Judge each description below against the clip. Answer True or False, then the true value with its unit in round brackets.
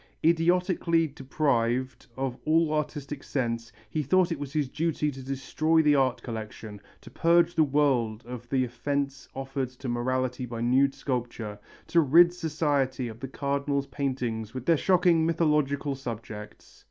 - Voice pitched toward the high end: False (135 Hz)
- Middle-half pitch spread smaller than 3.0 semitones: False (3.7 semitones)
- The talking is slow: False (145 wpm)